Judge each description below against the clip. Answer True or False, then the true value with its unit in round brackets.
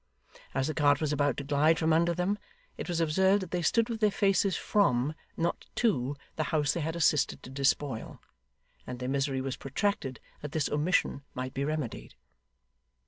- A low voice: False (150 Hz)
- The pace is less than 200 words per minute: True (185 wpm)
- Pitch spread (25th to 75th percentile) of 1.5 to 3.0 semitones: False (4.3 semitones)